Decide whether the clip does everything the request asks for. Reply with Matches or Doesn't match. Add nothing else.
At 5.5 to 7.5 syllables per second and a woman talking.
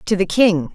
Doesn't match